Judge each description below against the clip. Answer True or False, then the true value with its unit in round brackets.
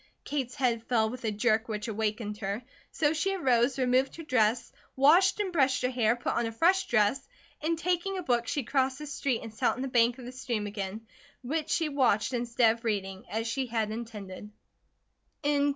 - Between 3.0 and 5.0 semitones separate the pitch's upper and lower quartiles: True (3.7 semitones)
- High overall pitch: True (245 Hz)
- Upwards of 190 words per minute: True (200 wpm)